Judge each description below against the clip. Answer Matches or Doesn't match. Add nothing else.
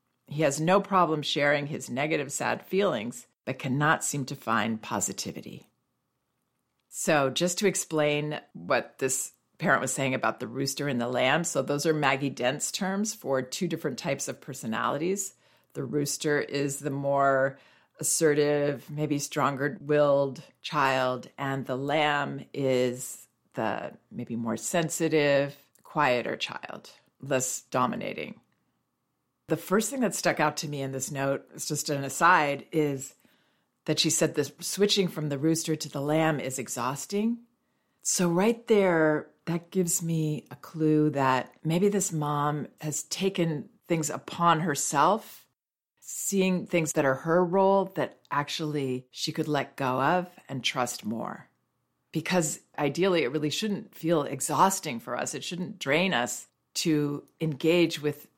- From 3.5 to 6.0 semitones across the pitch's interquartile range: Matches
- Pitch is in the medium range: Matches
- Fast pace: Doesn't match